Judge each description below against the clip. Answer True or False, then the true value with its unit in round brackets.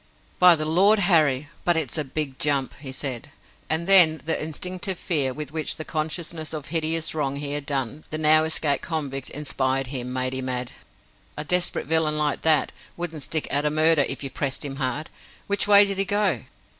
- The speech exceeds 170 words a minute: True (200 wpm)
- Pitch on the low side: False (155 Hz)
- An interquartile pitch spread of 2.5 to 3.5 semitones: True (2.8 semitones)